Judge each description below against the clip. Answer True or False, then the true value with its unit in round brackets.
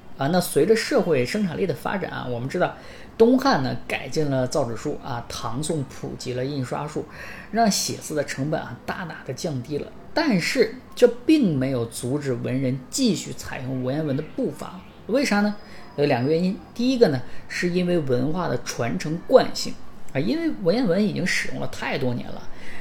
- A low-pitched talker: False (160 Hz)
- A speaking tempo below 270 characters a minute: False (275 characters per minute)